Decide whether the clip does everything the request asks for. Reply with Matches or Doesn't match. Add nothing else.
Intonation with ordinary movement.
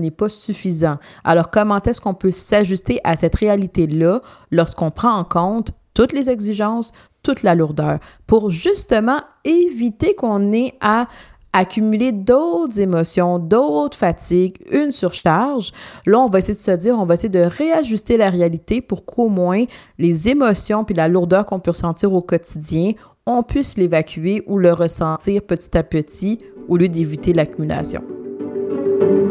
Matches